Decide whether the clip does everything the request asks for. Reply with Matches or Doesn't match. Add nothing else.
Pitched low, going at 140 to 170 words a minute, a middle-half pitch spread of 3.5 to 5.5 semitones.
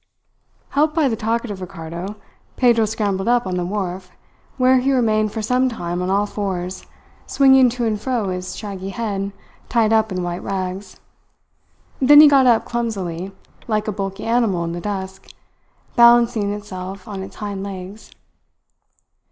Doesn't match